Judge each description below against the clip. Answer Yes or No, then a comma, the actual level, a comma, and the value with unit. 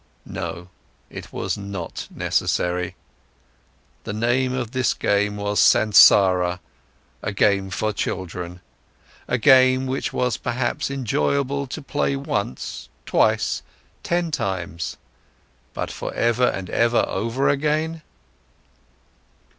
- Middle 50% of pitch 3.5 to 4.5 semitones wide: No, wide, 5.5 semitones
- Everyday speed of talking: No, slow, 105 wpm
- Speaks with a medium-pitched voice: No, low, 115 Hz